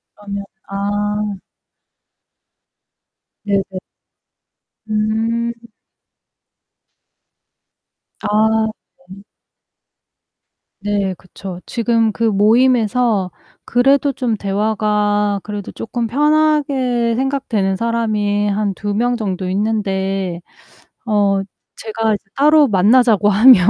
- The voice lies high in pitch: Yes, high, 210 Hz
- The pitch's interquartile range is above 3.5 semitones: No, average, 2.8 semitones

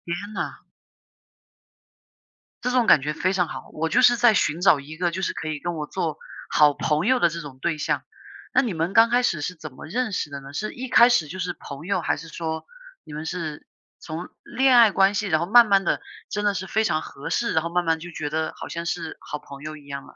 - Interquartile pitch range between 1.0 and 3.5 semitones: No, average, 4.7 semitones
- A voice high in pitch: No, medium, 170 Hz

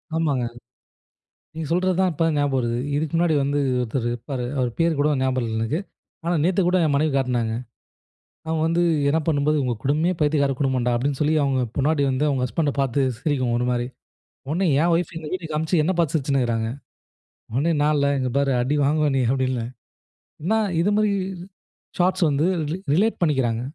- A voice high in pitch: No, medium, 145 Hz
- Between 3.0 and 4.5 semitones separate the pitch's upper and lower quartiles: Yes, average, 3.9 semitones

